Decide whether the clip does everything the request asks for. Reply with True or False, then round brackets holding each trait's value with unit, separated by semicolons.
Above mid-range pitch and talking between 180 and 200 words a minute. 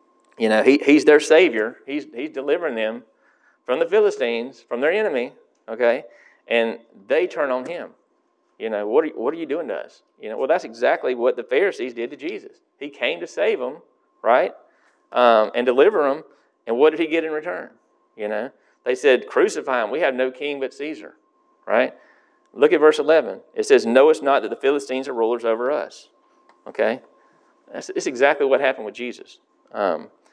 True (285 Hz; 195 wpm)